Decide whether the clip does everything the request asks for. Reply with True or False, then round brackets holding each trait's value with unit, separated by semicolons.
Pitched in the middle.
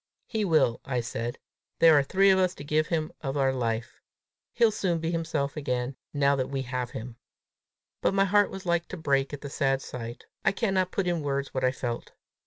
True (145 Hz)